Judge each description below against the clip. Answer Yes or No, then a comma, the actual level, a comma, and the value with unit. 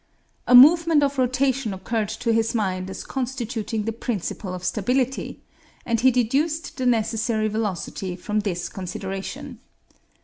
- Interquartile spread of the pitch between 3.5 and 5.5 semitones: Yes, average, 4.0 semitones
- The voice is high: Yes, high, 225 Hz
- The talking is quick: No, slow, 135 wpm